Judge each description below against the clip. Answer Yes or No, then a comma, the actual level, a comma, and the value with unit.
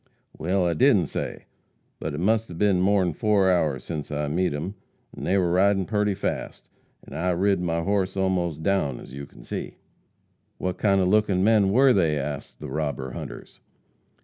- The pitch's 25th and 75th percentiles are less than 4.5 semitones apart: Yes, average, 4.0 semitones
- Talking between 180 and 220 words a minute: Yes, average, 185 wpm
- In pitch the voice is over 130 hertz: No, very low, 90 Hz